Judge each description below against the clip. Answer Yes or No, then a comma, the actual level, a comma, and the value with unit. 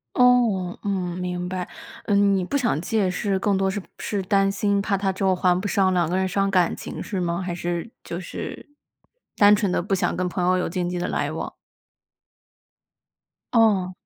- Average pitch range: No, narrow, 2.0 semitones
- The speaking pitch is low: No, high, 190 Hz